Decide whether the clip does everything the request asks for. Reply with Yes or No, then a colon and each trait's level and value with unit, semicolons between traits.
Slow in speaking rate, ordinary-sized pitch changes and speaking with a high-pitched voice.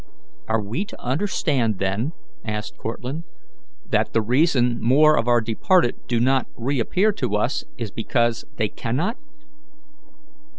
No: slow, 130 wpm; average, 4.2 semitones; low, 120 Hz